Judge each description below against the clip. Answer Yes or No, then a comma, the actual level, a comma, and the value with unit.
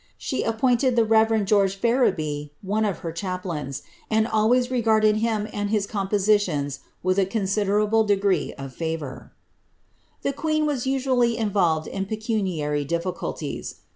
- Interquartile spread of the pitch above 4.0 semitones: No, average, 3.6 semitones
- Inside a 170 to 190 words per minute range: No, slow, 135 wpm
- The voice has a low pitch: No, high, 205 Hz